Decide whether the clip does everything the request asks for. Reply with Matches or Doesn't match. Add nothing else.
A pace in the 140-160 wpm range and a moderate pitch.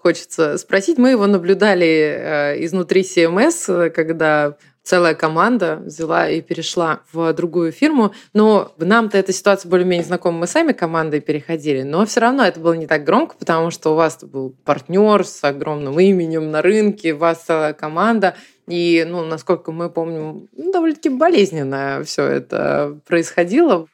Matches